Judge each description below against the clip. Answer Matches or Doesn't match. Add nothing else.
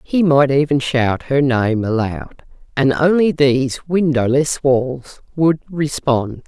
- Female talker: Matches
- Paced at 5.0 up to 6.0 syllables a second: Doesn't match